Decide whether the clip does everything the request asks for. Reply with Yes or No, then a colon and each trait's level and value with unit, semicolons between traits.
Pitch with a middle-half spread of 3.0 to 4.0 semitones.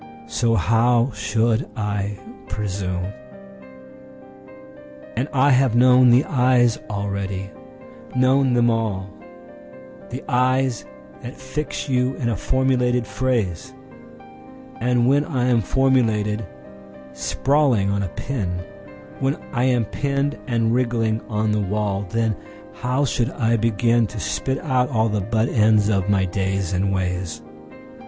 No: average, 4.6 semitones